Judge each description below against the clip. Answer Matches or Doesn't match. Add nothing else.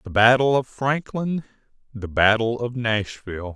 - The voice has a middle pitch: Doesn't match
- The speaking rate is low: Matches